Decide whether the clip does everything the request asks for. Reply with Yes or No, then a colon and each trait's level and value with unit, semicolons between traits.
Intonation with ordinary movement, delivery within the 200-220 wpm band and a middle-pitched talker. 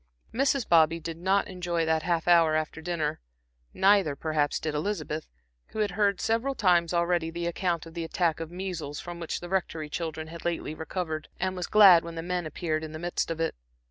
No: narrow, 2.2 semitones; fast, 205 wpm; medium, 170 Hz